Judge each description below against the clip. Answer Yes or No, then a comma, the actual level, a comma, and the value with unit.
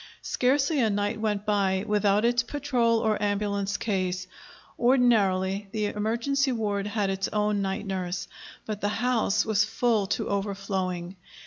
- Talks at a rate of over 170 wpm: No, average, 140 wpm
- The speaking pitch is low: No, high, 205 Hz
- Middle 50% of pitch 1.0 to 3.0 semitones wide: Yes, average, 2.7 semitones